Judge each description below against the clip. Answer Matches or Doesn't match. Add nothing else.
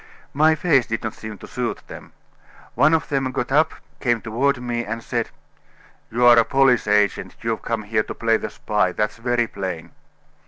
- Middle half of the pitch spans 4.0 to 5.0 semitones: Doesn't match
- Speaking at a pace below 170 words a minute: Doesn't match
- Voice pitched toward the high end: Doesn't match